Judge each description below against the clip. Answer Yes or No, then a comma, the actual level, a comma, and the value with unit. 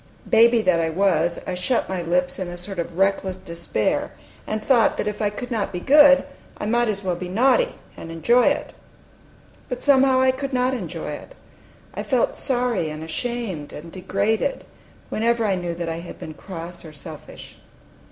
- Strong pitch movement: Yes, wide, 5.8 semitones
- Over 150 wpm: Yes, average, 185 wpm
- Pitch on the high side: Yes, high, 200 Hz